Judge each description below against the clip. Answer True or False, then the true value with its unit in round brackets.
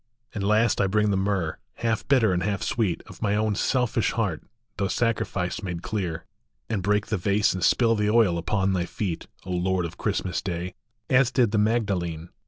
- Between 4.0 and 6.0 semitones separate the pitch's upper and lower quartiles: False (3.3 semitones)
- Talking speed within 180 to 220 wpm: True (190 wpm)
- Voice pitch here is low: True (100 Hz)